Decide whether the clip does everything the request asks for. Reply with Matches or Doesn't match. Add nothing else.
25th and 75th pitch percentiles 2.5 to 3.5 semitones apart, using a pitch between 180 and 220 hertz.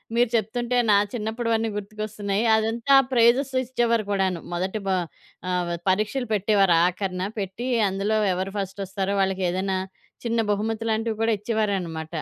Matches